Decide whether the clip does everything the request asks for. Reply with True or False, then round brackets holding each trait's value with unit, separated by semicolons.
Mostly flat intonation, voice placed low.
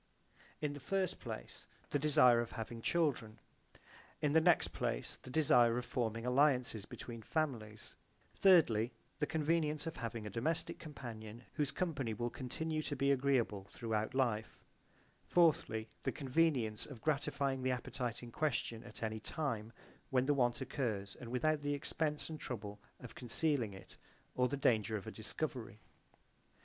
False (4.7 semitones; 125 Hz)